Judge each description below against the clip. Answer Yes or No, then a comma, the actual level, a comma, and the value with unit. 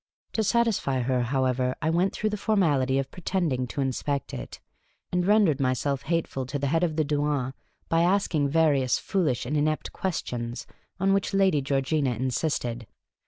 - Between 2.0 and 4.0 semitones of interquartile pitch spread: No, average, 5.1 semitones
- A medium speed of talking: Yes, average, 165 wpm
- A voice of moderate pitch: Yes, medium, 145 Hz